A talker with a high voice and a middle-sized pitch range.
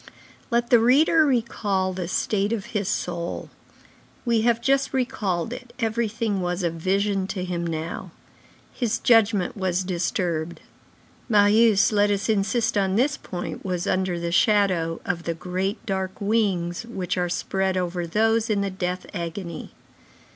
Yes: high, 195 Hz; average, 4.0 semitones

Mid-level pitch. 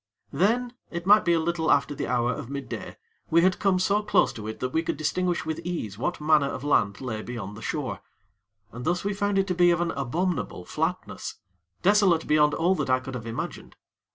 Yes: medium, 160 Hz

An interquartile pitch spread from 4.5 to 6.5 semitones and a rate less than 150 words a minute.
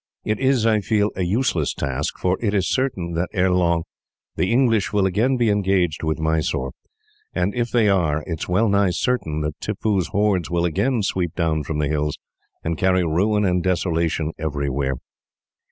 No: average, 4.8 semitones; average, 180 wpm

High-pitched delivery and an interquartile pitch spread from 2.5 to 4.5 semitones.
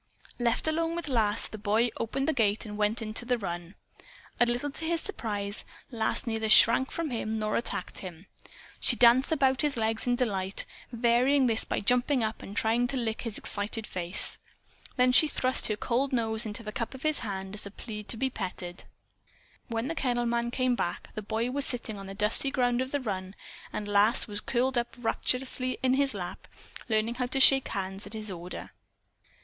Yes: high, 230 Hz; average, 3.4 semitones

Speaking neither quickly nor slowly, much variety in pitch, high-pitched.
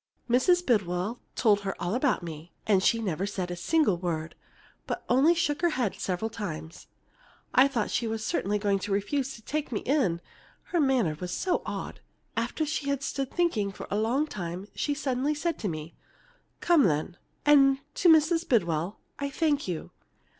Yes: average, 175 wpm; wide, 7.5 semitones; high, 230 Hz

